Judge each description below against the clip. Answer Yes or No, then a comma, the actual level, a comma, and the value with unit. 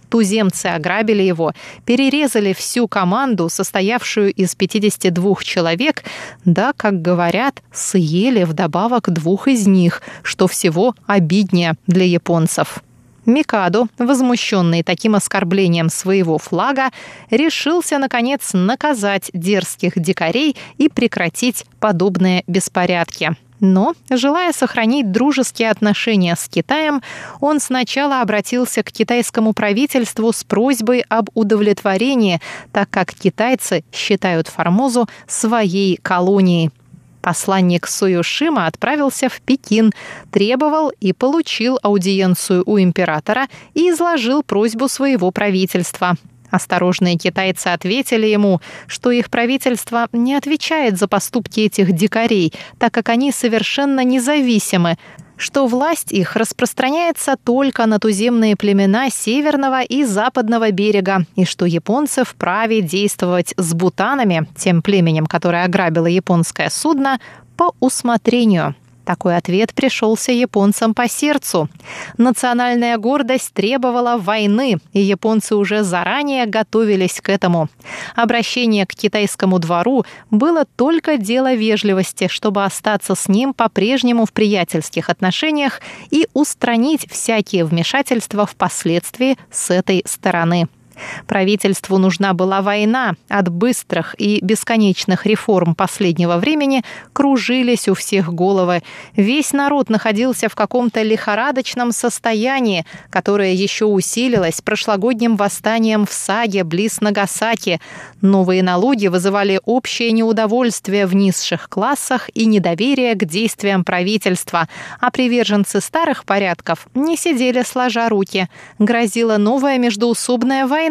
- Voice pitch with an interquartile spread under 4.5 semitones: No, average, 4.9 semitones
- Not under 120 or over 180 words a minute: No, slow, 110 wpm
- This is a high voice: Yes, high, 210 Hz